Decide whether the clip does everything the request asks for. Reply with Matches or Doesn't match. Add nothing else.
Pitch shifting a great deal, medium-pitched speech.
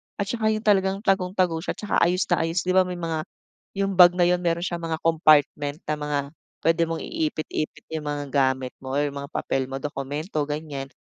Doesn't match